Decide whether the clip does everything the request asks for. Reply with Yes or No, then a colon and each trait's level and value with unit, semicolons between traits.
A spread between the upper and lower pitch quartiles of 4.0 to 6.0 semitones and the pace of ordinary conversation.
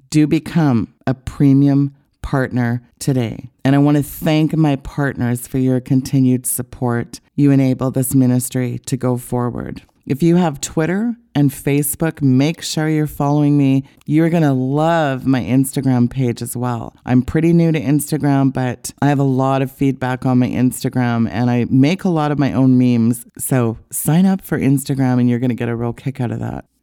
No: narrow, 2.6 semitones; average, 190 wpm